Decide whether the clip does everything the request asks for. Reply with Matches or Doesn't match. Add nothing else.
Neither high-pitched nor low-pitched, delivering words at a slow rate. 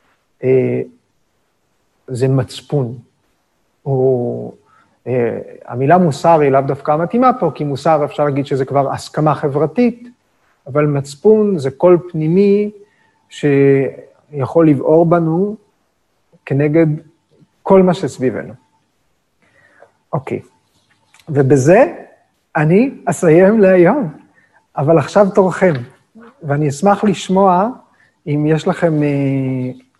Matches